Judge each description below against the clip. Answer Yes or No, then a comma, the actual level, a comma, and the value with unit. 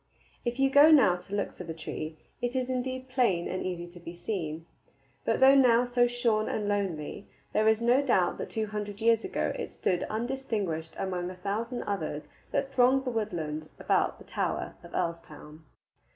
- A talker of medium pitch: No, high, 210 Hz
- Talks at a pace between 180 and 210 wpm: Yes, average, 185 wpm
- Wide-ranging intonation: Yes, wide, 6.0 semitones